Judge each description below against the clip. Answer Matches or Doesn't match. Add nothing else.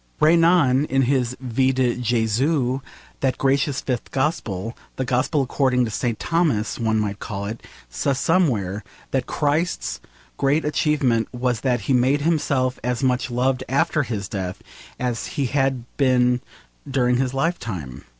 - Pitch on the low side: Matches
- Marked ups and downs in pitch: Doesn't match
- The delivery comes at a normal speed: Matches